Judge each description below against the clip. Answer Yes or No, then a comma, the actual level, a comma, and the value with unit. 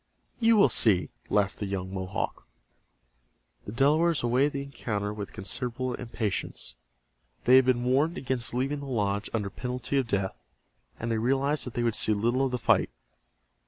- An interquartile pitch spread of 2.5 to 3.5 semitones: No, average, 4.5 semitones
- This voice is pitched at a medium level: No, low, 120 Hz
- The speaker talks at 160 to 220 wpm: Yes, average, 165 wpm